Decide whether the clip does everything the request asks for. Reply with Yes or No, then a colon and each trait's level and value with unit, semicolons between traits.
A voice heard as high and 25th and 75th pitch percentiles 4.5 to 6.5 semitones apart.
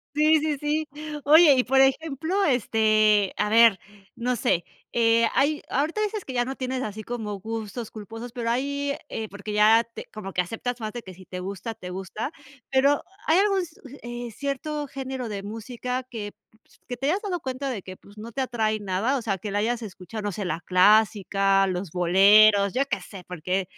Yes: high, 230 Hz; average, 4.8 semitones